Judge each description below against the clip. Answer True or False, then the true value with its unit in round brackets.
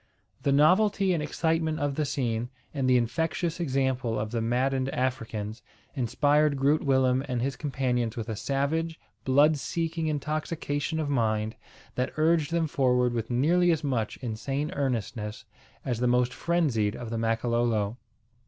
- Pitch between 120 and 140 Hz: True (135 Hz)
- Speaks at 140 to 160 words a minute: True (150 wpm)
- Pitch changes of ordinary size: True (4.4 semitones)